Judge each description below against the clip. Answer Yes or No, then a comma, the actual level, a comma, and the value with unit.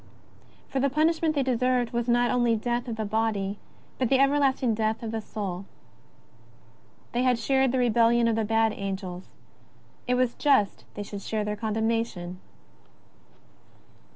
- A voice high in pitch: Yes, high, 230 Hz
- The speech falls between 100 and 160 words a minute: Yes, average, 155 wpm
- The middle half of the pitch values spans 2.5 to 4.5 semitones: Yes, average, 2.9 semitones